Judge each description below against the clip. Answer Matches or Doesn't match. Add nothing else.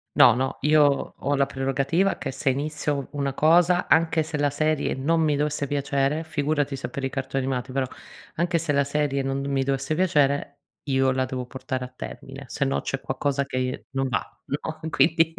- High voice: Doesn't match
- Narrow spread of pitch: Matches